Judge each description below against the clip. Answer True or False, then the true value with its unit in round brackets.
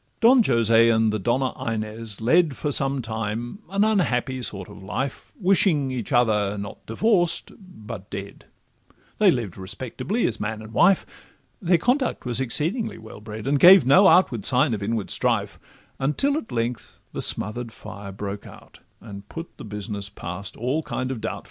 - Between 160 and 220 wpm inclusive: True (165 wpm)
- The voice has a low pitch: True (120 Hz)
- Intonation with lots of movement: True (7.0 semitones)